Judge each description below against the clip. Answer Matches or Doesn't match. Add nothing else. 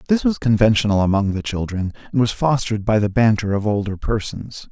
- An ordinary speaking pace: Matches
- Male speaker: Matches